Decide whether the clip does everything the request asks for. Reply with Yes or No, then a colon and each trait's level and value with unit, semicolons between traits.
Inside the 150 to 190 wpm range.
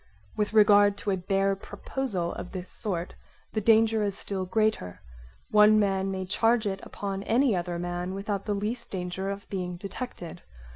Yes: average, 165 wpm